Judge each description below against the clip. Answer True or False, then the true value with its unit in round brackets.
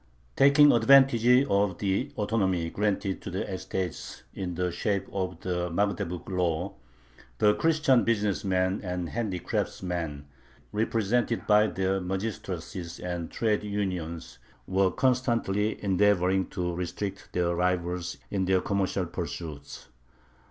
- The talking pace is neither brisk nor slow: False (115 wpm)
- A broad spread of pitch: False (2.8 semitones)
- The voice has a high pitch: False (95 Hz)